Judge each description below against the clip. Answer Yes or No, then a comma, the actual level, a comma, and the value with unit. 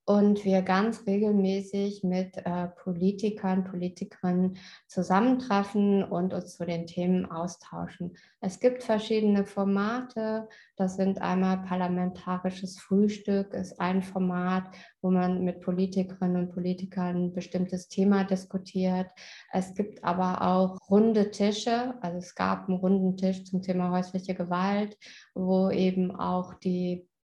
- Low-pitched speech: No, medium, 185 Hz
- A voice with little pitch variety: Yes, narrow, 1.6 semitones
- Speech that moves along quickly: No, slow, 125 wpm